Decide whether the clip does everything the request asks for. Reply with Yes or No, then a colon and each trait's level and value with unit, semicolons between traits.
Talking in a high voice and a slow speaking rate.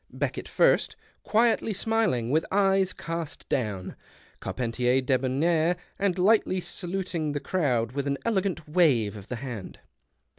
No: medium, 155 Hz; slow, 125 wpm